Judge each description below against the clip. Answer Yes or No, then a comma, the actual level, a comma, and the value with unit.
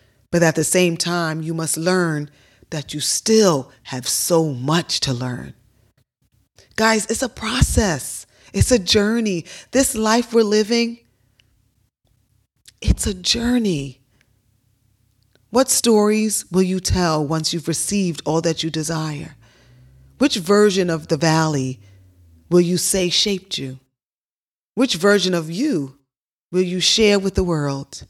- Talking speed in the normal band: No, slow, 130 wpm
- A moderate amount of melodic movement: No, wide, 7.4 semitones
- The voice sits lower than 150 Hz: No, medium, 165 Hz